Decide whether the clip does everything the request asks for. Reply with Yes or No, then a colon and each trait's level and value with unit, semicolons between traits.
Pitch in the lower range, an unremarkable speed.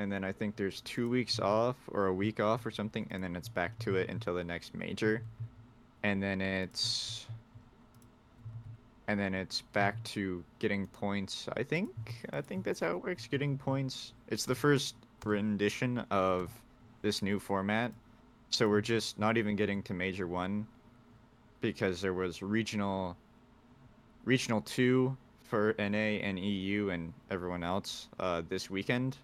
Yes: low, 110 Hz; average, 160 wpm